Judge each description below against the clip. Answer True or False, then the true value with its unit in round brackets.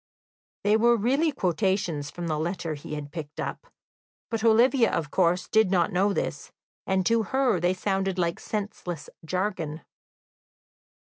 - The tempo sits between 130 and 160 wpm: True (145 wpm)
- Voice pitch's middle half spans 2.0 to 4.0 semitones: False (4.5 semitones)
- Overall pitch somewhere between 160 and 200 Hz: True (190 Hz)